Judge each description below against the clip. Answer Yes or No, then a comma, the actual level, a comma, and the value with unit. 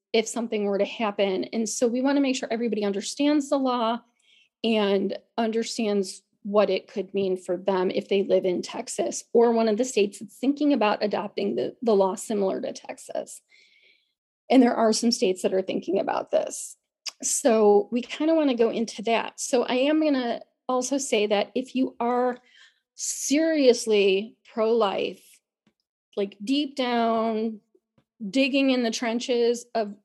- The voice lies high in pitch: Yes, high, 230 Hz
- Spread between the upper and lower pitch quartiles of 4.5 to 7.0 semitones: No, average, 3.5 semitones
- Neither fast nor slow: Yes, average, 170 wpm